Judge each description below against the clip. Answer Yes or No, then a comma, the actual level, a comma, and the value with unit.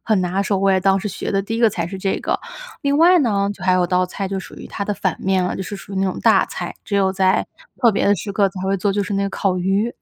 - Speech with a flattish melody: Yes, narrow, 1.3 semitones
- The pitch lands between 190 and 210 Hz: Yes, high, 195 Hz